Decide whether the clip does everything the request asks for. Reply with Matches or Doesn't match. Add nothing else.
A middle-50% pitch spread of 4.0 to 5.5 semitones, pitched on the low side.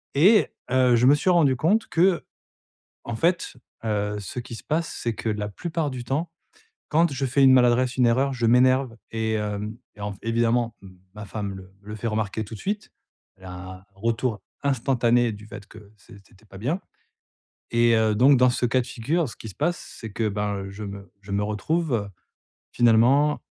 Matches